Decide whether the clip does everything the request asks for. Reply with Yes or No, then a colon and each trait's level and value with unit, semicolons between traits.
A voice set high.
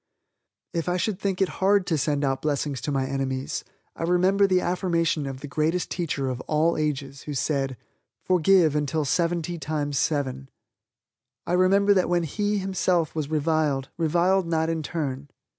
No: medium, 160 Hz